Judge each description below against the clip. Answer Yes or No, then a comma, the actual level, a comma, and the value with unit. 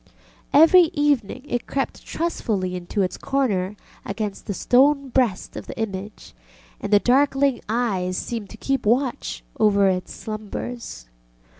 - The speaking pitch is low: No, high, 225 Hz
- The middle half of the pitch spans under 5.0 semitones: No, average, 5.3 semitones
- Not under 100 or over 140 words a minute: Yes, slow, 135 wpm